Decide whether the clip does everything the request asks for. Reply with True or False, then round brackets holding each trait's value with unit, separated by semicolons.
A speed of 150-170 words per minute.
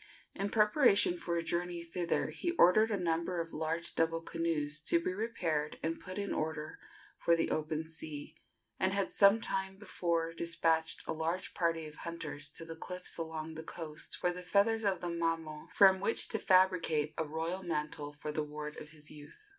False (185 wpm)